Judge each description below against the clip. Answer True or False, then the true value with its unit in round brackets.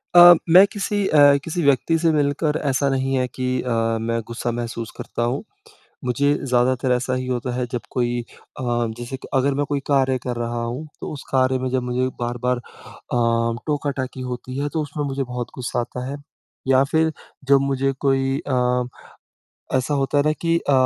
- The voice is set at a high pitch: False (130 Hz)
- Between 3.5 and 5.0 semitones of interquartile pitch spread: False (2.4 semitones)